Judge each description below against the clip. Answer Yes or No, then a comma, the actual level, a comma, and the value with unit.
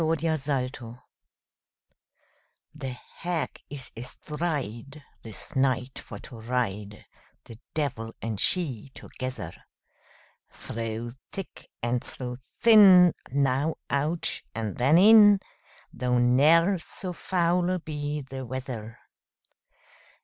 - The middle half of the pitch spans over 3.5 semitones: Yes, average, 5.2 semitones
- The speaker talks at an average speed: No, slow, 100 wpm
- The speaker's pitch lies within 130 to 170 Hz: Yes, low, 135 Hz